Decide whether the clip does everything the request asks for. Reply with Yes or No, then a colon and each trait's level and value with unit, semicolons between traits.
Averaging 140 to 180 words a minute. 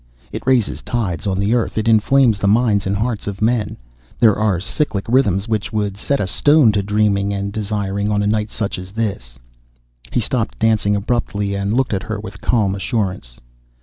No: average, 190 wpm